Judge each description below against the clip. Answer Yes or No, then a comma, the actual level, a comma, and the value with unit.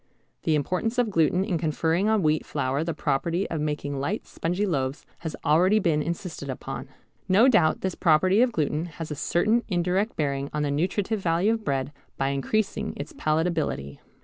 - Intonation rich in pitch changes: No, average, 4.3 semitones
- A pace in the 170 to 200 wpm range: Yes, average, 175 wpm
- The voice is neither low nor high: Yes, medium, 165 Hz